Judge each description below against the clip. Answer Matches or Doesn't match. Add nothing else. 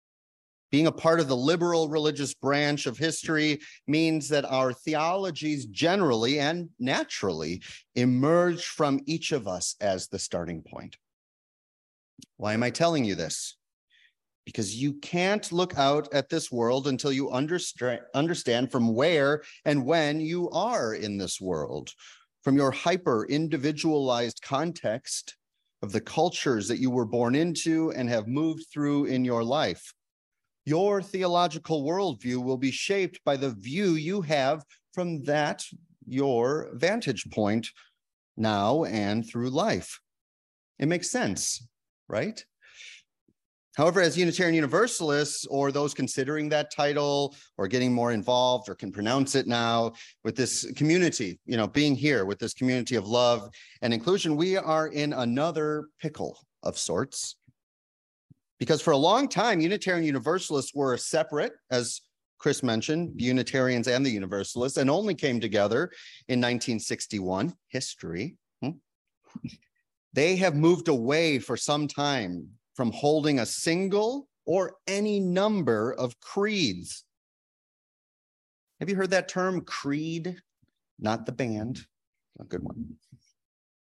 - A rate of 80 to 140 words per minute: Matches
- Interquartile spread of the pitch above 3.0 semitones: Matches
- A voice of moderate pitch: Matches